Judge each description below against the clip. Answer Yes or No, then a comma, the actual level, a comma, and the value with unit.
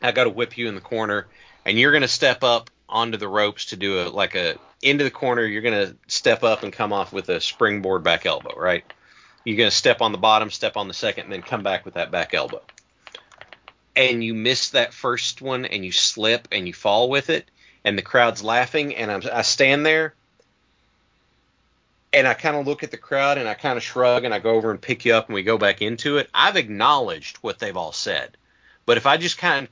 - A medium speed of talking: No, fast, 240 wpm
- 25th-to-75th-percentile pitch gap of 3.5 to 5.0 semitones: Yes, average, 4.0 semitones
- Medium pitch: No, low, 120 Hz